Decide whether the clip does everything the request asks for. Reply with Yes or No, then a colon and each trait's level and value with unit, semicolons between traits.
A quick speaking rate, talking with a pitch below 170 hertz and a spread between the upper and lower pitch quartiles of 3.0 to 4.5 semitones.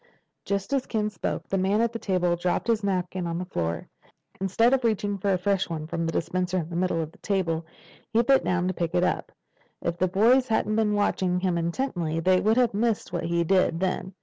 No: fast, 230 wpm; medium, 185 Hz; average, 3.4 semitones